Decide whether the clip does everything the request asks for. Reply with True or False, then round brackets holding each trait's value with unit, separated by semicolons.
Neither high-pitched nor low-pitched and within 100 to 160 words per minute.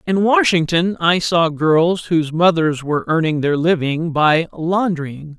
True (165 Hz; 145 wpm)